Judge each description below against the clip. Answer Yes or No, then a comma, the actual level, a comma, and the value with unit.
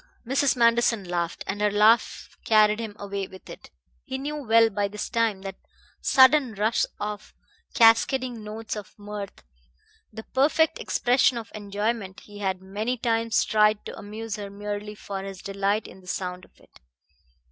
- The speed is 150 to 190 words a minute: Yes, average, 160 wpm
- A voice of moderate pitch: No, high, 210 Hz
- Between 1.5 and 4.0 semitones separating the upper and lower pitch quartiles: Yes, narrow, 2.4 semitones